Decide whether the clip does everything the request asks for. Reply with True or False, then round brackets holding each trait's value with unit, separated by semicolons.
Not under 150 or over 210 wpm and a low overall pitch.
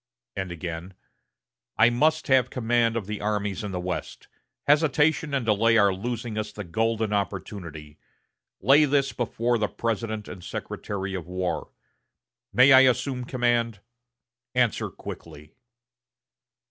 False (135 wpm; 110 Hz)